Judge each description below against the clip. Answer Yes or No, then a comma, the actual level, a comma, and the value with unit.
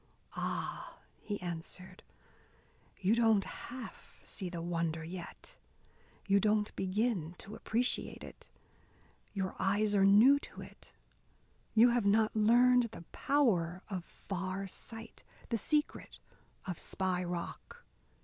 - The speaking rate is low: Yes, slow, 120 wpm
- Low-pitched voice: No, high, 200 Hz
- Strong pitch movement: No, average, 3.7 semitones